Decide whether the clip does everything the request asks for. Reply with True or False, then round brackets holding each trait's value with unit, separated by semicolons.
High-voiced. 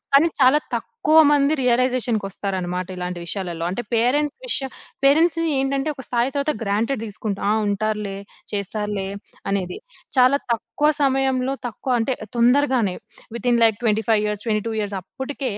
True (235 Hz)